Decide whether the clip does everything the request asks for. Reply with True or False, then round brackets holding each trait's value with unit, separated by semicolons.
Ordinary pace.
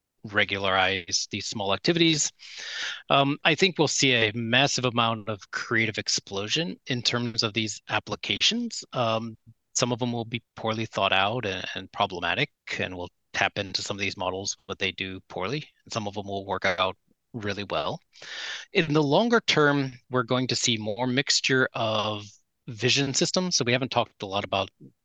True (175 wpm)